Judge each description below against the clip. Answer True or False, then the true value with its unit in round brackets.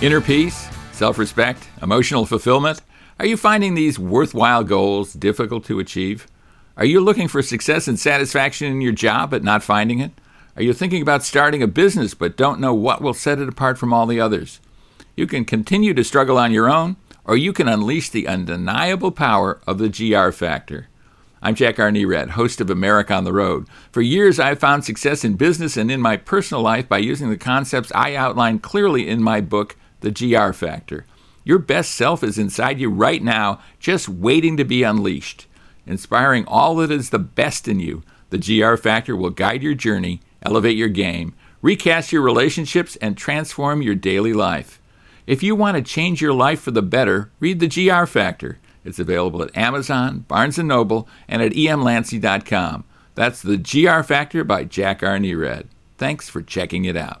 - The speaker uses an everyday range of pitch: False (6.0 semitones)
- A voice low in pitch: True (120 Hz)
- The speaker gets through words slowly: False (185 wpm)